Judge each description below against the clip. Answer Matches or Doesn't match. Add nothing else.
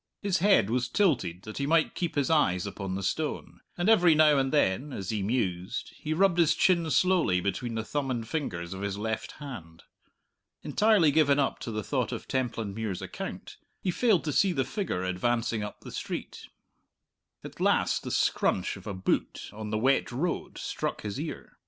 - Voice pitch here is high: Doesn't match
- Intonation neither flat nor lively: Doesn't match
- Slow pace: Doesn't match